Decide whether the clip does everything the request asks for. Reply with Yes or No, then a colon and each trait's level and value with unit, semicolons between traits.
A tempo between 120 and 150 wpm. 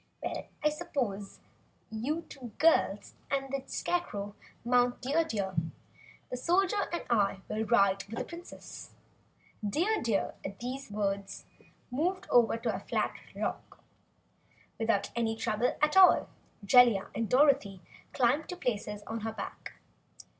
Yes: average, 140 wpm